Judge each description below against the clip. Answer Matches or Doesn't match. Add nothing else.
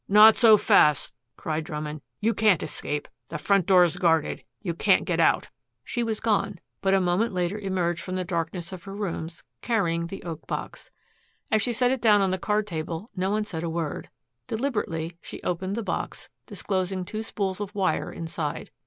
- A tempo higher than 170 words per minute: Matches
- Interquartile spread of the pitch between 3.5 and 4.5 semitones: Matches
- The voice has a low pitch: Doesn't match